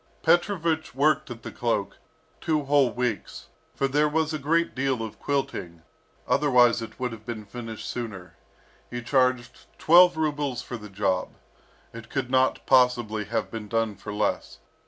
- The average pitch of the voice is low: Yes, low, 125 Hz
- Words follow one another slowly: No, average, 155 wpm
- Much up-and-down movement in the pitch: No, average, 4.6 semitones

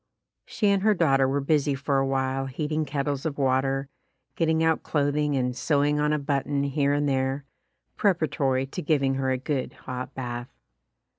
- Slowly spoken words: No, average, 170 wpm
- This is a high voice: No, medium, 140 Hz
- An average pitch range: No, narrow, 1.9 semitones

